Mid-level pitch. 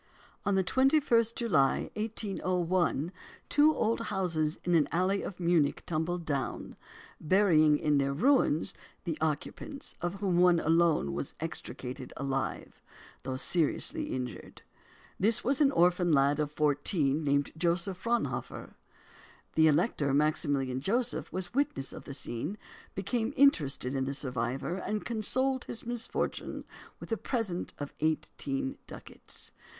Yes: medium, 170 Hz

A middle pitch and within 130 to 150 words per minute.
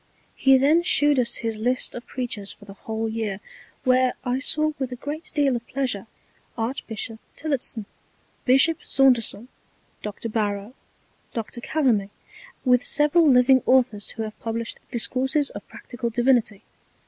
No: high, 245 Hz; average, 140 wpm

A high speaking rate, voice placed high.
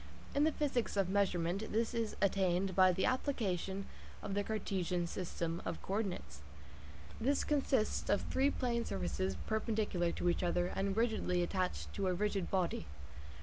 No: average, 155 wpm; high, 195 Hz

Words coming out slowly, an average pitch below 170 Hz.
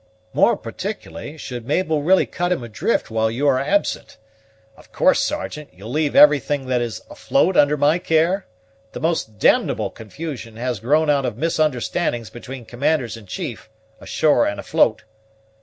No: average, 155 wpm; medium, 140 Hz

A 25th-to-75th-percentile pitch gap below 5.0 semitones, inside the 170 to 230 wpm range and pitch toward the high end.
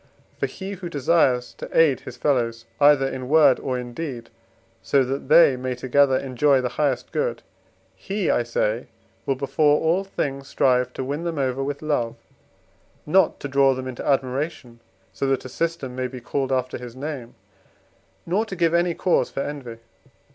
No: average, 3.4 semitones; average, 175 wpm; low, 135 Hz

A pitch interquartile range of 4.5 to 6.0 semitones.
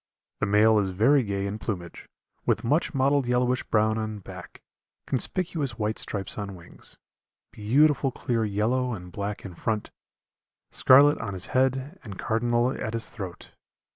No: average, 4.1 semitones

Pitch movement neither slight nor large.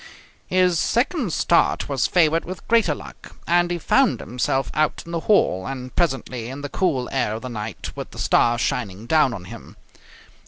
No: wide, 6.1 semitones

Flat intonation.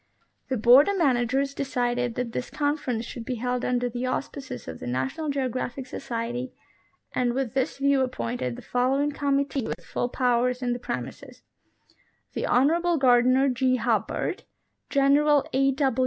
Yes: narrow, 2.3 semitones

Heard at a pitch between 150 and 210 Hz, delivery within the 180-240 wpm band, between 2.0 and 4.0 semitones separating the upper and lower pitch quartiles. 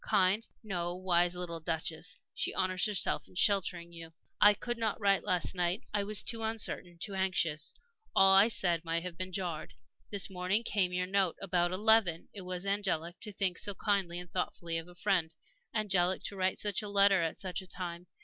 Yes: medium, 185 Hz; average, 190 wpm; narrow, 2.5 semitones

